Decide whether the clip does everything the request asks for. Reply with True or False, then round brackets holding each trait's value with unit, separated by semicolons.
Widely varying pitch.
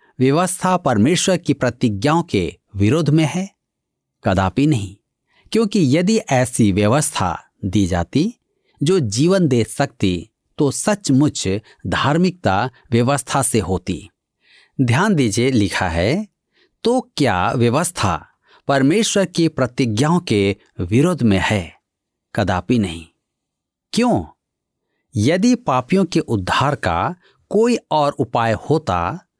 True (8.0 semitones)